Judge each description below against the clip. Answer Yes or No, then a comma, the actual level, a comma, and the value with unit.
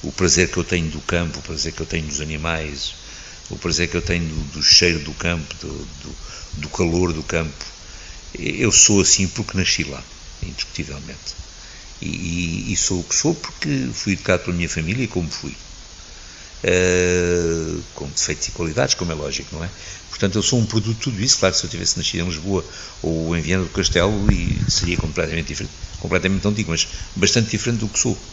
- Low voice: Yes, very low, 85 Hz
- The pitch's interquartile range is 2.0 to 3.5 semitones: Yes, average, 3.0 semitones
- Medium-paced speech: No, fast, 200 wpm